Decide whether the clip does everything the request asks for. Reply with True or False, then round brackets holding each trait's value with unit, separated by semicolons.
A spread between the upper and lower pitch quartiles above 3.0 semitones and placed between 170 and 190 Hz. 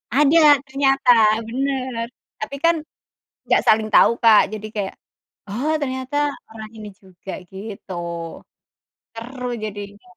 False (4.2 semitones; 230 Hz)